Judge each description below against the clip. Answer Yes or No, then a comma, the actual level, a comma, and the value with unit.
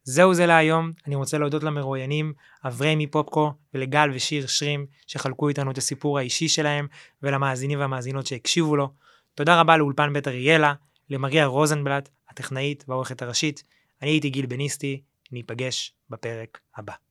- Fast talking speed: No, average, 135 wpm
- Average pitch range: No, narrow, 2.0 semitones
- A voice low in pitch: No, medium, 145 Hz